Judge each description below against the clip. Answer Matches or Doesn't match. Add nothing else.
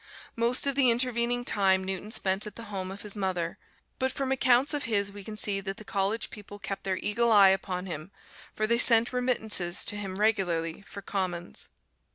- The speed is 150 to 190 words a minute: Doesn't match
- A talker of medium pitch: Doesn't match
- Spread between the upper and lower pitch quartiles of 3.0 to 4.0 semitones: Matches